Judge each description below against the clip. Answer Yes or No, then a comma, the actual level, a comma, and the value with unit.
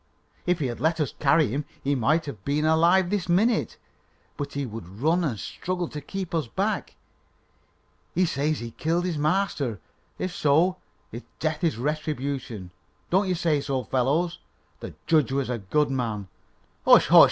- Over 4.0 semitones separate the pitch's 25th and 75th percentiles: Yes, average, 4.7 semitones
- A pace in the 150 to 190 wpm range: Yes, average, 175 wpm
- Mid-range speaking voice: Yes, medium, 150 Hz